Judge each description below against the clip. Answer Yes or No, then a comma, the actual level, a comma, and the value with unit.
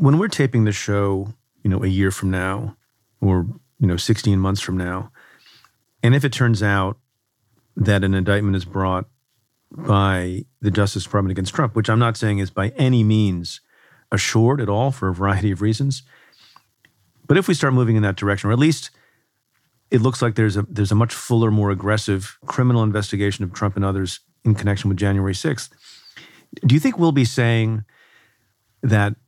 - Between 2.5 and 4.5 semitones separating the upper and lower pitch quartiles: Yes, average, 3.3 semitones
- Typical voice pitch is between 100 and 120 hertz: Yes, low, 105 Hz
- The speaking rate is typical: Yes, average, 185 wpm